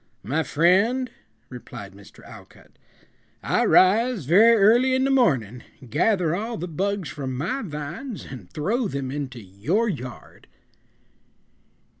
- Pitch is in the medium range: Yes, medium, 175 Hz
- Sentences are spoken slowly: Yes, slow, 125 wpm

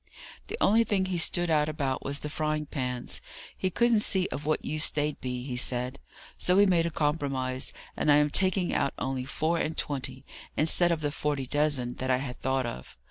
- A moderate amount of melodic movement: Yes, average, 4.1 semitones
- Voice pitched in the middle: Yes, medium, 150 Hz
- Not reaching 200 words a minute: No, fast, 205 wpm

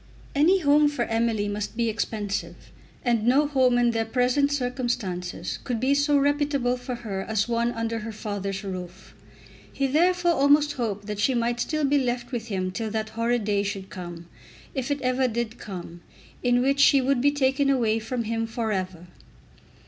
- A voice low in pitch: No, high, 240 Hz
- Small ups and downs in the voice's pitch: No, average, 4.3 semitones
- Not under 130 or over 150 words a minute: No, average, 180 wpm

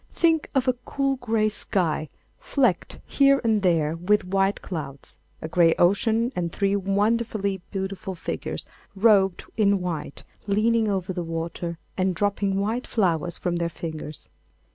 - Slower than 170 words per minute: Yes, average, 140 wpm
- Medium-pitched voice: No, high, 195 Hz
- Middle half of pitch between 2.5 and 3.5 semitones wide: No, average, 4.1 semitones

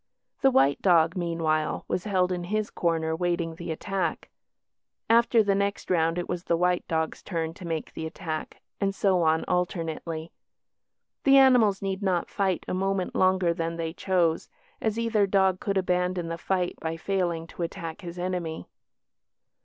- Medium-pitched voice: Yes, medium, 180 Hz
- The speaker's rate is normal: Yes, average, 165 wpm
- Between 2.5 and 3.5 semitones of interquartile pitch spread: Yes, average, 2.8 semitones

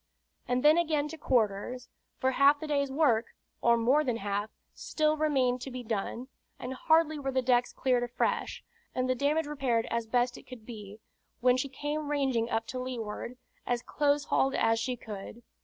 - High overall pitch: Yes, very high, 255 Hz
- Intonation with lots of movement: No, average, 3.6 semitones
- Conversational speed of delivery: Yes, average, 180 wpm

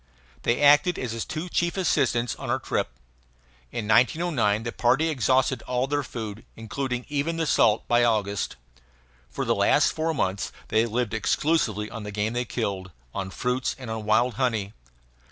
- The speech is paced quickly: No, average, 170 wpm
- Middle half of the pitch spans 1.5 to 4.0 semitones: No, average, 4.4 semitones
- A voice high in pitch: No, low, 120 Hz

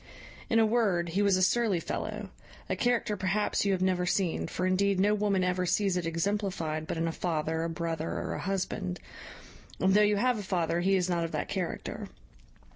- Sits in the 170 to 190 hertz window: Yes, medium, 185 Hz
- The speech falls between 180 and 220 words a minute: Yes, fast, 205 wpm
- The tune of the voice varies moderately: Yes, average, 3.1 semitones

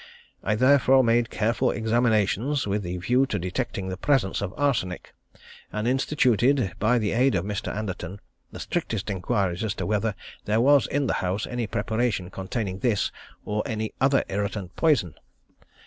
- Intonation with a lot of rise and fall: No, average, 4.1 semitones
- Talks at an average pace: Yes, average, 160 wpm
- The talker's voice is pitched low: Yes, low, 110 Hz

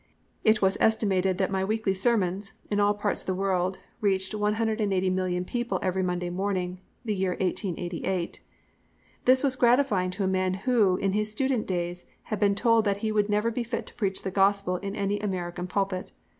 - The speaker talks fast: No, average, 185 wpm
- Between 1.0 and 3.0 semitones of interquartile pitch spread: Yes, narrow, 2.5 semitones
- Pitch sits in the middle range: No, high, 195 Hz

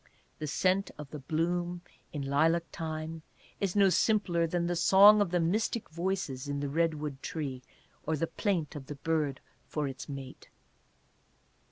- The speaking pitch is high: No, medium, 160 Hz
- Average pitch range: Yes, average, 3.4 semitones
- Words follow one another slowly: No, average, 160 wpm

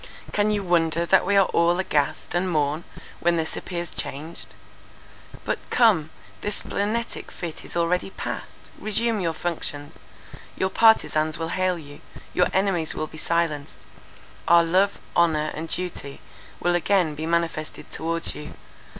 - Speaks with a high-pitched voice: No, medium, 170 Hz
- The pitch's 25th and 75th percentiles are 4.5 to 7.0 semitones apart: No, average, 3.0 semitones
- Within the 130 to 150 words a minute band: Yes, average, 140 wpm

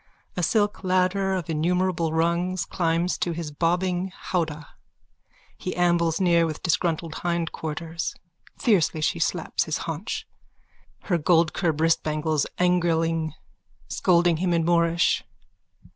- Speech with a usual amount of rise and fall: No, narrow, 1.8 semitones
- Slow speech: Yes, slow, 115 wpm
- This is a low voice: No, medium, 170 Hz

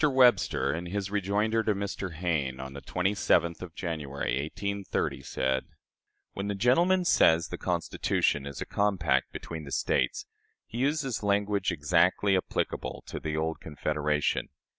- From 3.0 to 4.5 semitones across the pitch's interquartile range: No, average, 5.1 semitones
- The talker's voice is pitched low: Yes, very low, 90 Hz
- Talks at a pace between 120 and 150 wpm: Yes, average, 140 wpm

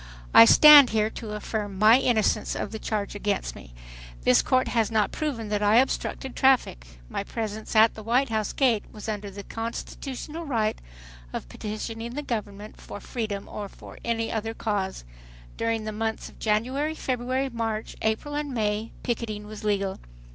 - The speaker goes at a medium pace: Yes, average, 170 wpm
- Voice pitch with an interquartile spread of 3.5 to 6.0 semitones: No, narrow, 2.6 semitones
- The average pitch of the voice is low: No, high, 220 Hz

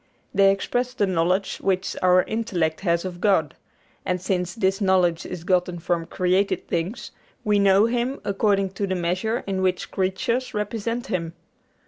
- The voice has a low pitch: No, high, 190 Hz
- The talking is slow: No, average, 155 wpm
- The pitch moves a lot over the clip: No, narrow, 2.5 semitones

